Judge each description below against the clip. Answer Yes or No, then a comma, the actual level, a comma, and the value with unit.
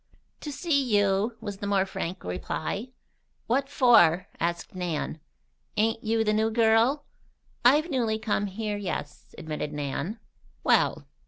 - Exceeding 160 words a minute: No, slow, 135 wpm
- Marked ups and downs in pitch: No, average, 4.1 semitones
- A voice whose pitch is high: Yes, high, 215 Hz